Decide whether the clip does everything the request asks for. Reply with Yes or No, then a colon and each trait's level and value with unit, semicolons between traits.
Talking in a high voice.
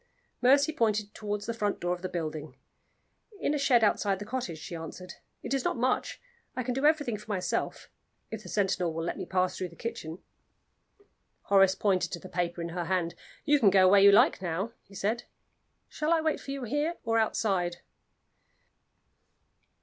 Yes: high, 200 Hz